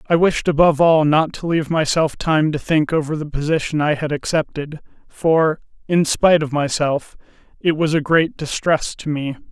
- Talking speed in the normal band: Yes, average, 185 wpm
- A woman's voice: No, male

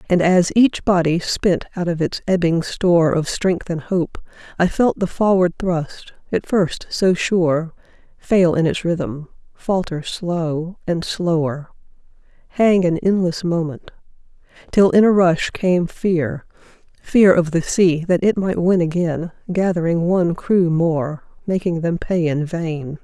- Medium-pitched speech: Yes, medium, 170 Hz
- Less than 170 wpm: Yes, average, 155 wpm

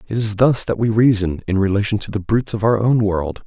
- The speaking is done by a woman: No, male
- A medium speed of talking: No, fast, 260 wpm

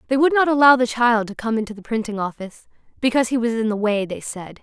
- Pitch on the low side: No, high, 235 Hz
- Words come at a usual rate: No, fast, 260 wpm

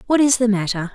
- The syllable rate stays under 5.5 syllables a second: No, 6.3 syllables/s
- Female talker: Yes, female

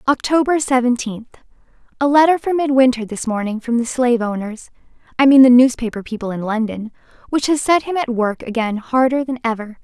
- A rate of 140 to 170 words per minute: Yes, average, 160 wpm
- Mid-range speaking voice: No, high, 245 Hz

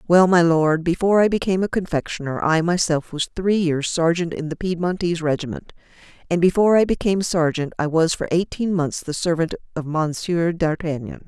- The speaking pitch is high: No, medium, 170 Hz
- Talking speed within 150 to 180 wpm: Yes, average, 175 wpm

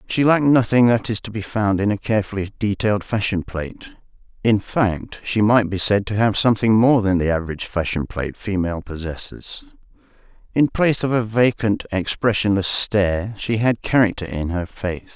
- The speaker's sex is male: Yes, male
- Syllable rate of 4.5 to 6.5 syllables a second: Yes, 5.4 syllables/s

